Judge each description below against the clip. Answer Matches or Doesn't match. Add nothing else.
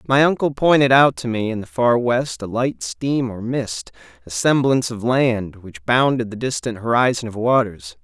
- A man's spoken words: Matches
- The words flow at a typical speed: Matches